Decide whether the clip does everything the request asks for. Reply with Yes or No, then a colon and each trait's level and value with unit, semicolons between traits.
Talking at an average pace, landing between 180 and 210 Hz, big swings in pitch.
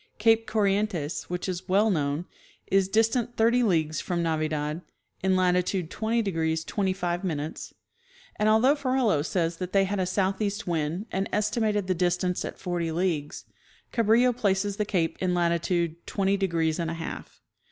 No: average, 150 wpm; medium, 185 Hz; average, 3.8 semitones